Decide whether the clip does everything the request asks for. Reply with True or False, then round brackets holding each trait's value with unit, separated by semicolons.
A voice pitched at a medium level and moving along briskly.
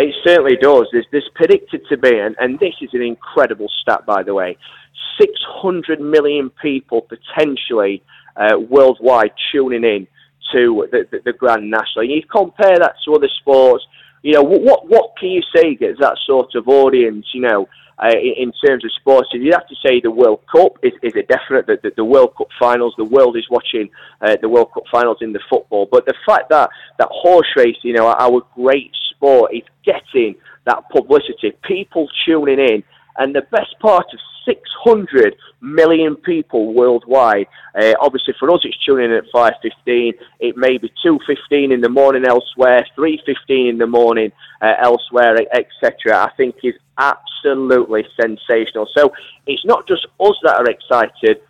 False (155 Hz; 175 wpm)